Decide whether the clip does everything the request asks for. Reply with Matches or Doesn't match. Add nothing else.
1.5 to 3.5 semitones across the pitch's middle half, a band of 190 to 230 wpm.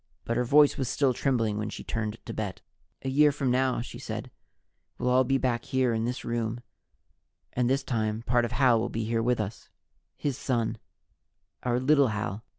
Matches